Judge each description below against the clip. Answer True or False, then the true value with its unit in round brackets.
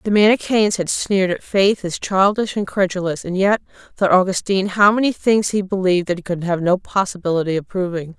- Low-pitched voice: False (190 Hz)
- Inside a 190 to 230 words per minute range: True (200 wpm)